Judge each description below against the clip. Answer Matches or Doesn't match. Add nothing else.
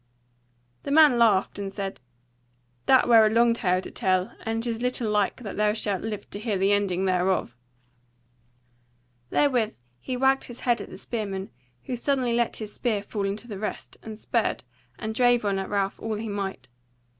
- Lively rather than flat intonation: Doesn't match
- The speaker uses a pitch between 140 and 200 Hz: Doesn't match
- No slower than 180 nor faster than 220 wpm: Matches